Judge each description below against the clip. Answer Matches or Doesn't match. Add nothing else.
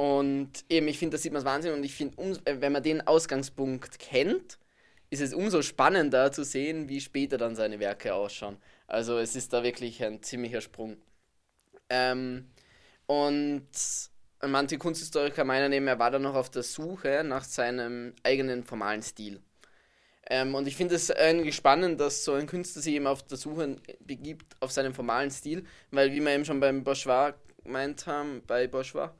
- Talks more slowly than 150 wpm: Doesn't match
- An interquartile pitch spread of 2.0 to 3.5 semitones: Matches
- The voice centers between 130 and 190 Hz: Matches